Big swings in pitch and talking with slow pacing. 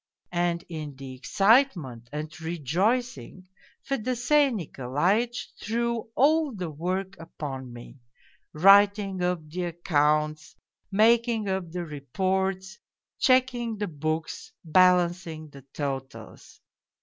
Yes: wide, 5.8 semitones; slow, 100 wpm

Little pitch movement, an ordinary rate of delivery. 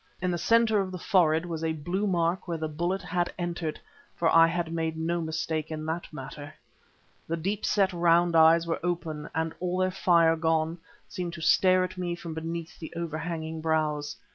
Yes: narrow, 1.7 semitones; average, 190 wpm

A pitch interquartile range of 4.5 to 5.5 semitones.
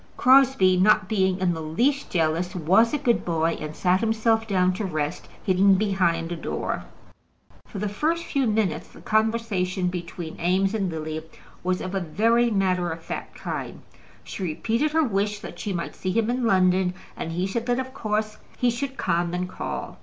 No: average, 4.0 semitones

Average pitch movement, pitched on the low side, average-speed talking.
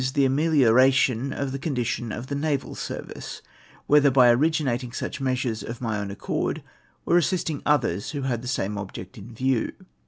Yes: average, 3.3 semitones; low, 130 Hz; average, 165 wpm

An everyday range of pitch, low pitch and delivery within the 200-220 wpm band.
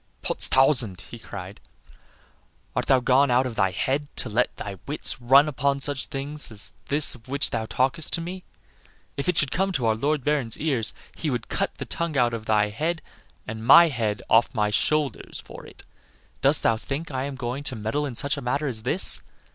Yes: average, 4.5 semitones; low, 130 Hz; fast, 205 wpm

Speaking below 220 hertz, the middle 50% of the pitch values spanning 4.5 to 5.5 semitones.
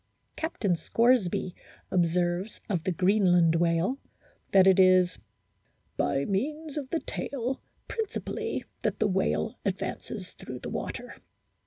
Yes: high, 190 Hz; average, 4.9 semitones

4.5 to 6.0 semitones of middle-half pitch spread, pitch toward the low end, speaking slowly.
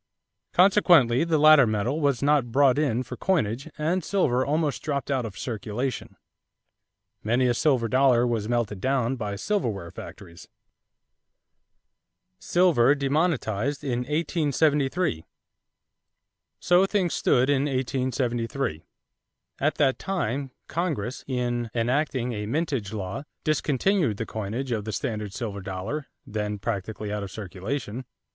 Yes: average, 5.0 semitones; low, 130 Hz; slow, 125 wpm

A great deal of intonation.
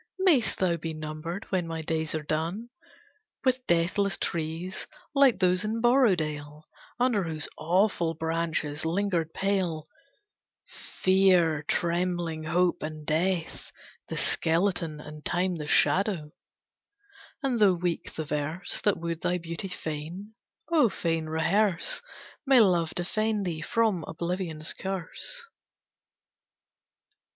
No: average, 3.7 semitones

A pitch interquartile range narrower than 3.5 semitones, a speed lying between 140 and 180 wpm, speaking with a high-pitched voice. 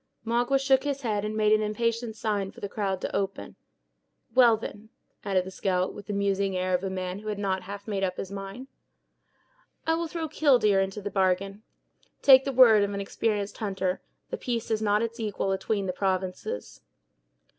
No: average, 2.9 semitones; average, 195 wpm; high, 205 Hz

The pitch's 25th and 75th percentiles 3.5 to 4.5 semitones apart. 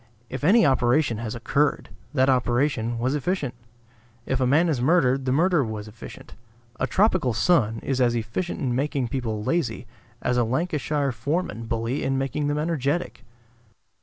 Yes: average, 4.0 semitones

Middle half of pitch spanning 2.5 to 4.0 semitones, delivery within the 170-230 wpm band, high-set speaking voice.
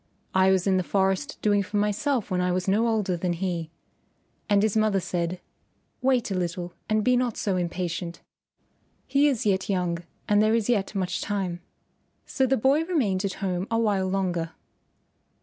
Yes: average, 3.1 semitones; average, 180 wpm; high, 195 Hz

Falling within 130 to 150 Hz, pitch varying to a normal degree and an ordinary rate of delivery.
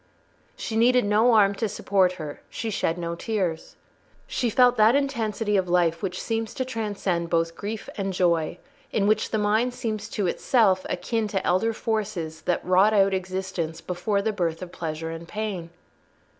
No: high, 200 Hz; average, 3.8 semitones; average, 170 wpm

